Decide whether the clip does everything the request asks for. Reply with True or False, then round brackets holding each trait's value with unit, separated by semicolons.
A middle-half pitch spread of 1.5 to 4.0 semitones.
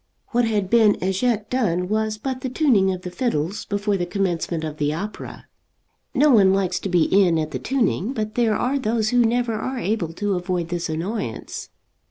False (4.6 semitones)